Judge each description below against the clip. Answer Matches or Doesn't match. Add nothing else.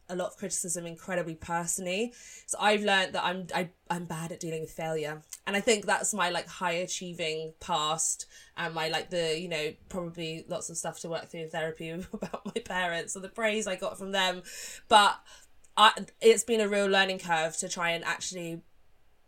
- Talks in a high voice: Doesn't match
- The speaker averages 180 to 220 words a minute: Matches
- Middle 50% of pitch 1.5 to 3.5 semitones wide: Matches